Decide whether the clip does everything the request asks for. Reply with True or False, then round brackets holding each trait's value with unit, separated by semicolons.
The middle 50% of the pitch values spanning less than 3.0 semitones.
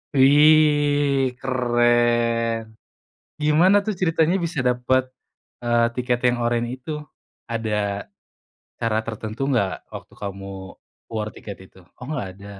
False (4.0 semitones)